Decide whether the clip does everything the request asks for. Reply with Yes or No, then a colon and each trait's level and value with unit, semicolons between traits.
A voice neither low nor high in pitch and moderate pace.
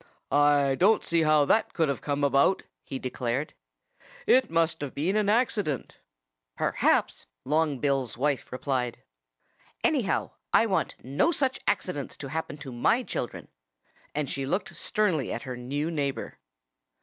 Yes: medium, 145 Hz; average, 145 wpm